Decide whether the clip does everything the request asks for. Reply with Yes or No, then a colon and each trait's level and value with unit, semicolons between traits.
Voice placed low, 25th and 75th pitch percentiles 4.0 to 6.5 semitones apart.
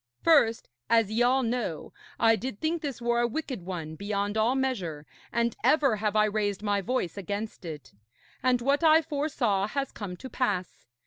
No: high, 225 Hz; average, 4.5 semitones